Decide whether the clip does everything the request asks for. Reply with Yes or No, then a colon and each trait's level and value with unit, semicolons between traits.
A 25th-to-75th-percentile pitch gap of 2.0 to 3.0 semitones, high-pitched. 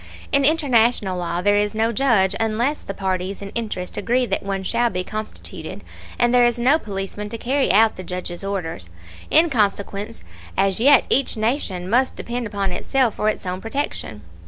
No: average, 3.9 semitones; high, 215 Hz